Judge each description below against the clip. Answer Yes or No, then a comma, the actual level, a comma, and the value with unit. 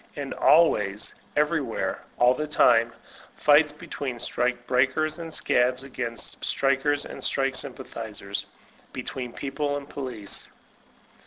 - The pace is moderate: No, slow, 115 wpm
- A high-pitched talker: No, low, 135 Hz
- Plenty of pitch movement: No, average, 3.2 semitones